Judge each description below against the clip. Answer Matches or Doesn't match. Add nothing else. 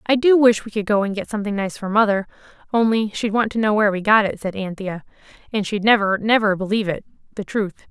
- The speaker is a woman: Matches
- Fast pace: Matches